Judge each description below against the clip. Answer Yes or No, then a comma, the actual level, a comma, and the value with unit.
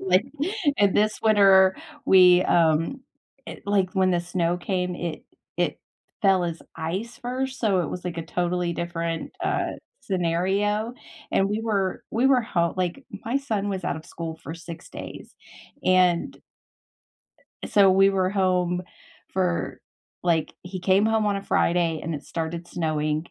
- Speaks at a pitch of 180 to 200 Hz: Yes, medium, 185 Hz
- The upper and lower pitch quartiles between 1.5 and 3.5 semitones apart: Yes, average, 2.8 semitones